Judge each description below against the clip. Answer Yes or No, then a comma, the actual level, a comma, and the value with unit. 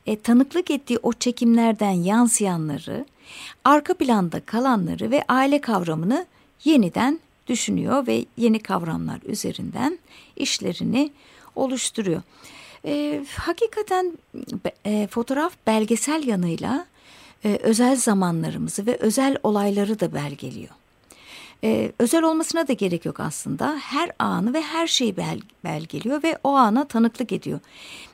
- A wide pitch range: Yes, wide, 5.9 semitones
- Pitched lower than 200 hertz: No, high, 235 Hz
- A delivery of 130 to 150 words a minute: No, average, 115 wpm